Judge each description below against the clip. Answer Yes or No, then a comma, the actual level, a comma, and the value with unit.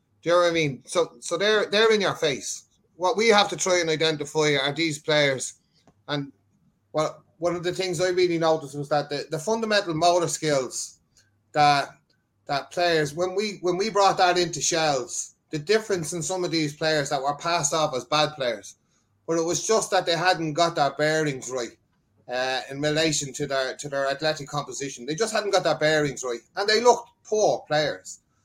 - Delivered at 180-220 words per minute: Yes, average, 200 wpm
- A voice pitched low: No, medium, 160 Hz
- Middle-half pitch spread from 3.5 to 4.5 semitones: Yes, average, 3.9 semitones